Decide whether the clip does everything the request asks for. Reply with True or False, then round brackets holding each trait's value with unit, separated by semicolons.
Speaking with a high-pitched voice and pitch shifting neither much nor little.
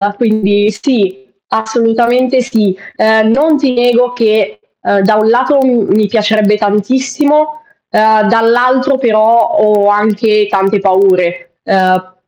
True (220 Hz; 3.2 semitones)